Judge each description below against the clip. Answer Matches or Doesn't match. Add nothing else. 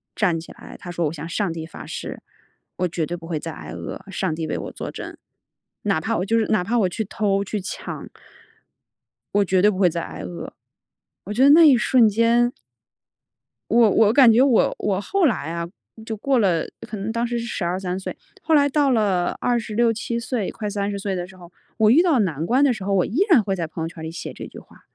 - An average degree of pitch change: Matches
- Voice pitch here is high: Matches